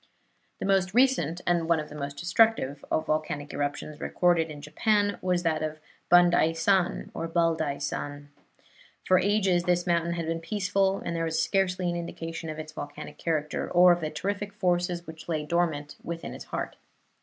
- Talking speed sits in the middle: Yes, average, 175 wpm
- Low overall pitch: No, medium, 170 Hz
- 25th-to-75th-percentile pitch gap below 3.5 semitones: Yes, average, 2.7 semitones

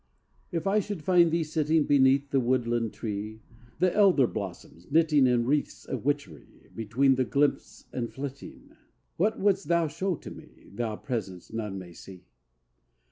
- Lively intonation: Yes, wide, 6.2 semitones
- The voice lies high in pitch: No, low, 135 Hz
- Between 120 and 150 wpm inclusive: No, average, 160 wpm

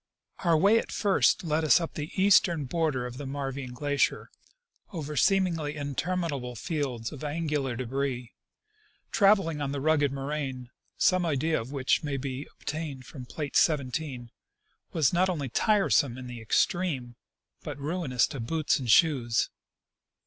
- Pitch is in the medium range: Yes, medium, 145 Hz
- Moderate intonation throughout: Yes, average, 4.0 semitones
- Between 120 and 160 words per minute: Yes, average, 140 wpm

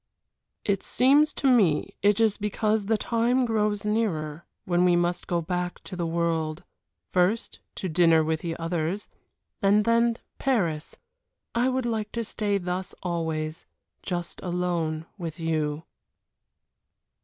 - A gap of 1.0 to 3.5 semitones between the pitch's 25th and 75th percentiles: No, average, 4.8 semitones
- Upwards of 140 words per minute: No, slow, 135 wpm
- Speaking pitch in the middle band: Yes, medium, 180 Hz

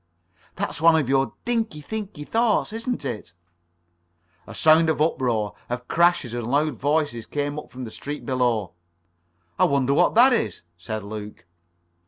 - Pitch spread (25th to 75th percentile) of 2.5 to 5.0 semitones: No, wide, 5.4 semitones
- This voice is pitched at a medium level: Yes, medium, 145 Hz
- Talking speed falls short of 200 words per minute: Yes, average, 160 wpm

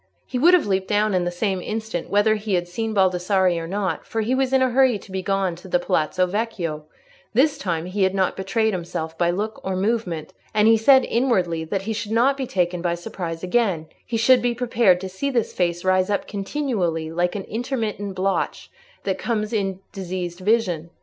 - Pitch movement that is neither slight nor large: Yes, average, 4.1 semitones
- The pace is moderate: No, fast, 210 wpm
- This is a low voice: No, high, 195 Hz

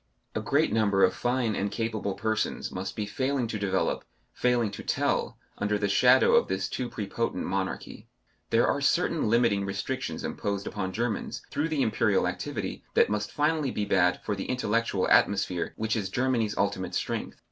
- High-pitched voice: No, low, 105 Hz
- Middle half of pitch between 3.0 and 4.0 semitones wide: Yes, average, 3.3 semitones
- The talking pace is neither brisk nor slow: Yes, average, 170 wpm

